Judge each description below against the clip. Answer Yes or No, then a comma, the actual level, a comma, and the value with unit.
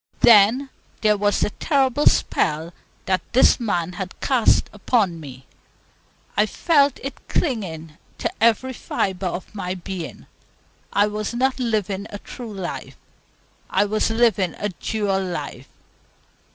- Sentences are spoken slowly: Yes, slow, 130 wpm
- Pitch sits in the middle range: No, high, 205 Hz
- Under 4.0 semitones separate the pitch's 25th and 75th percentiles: No, average, 4.5 semitones